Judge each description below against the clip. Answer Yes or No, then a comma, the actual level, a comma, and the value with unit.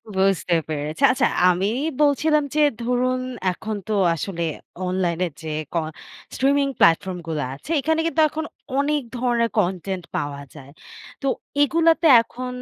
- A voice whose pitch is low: No, high, 220 Hz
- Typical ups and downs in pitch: No, wide, 8.3 semitones